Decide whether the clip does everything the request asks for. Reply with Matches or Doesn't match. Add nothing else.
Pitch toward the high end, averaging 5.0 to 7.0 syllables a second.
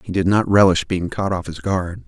Doesn't match